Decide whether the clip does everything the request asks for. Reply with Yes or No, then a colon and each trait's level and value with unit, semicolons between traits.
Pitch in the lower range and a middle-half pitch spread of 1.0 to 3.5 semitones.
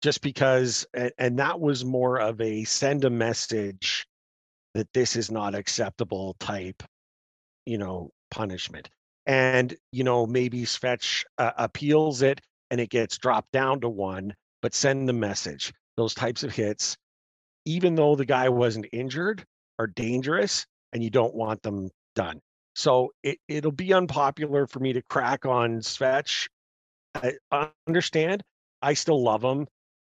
No: low, 125 Hz; average, 4.3 semitones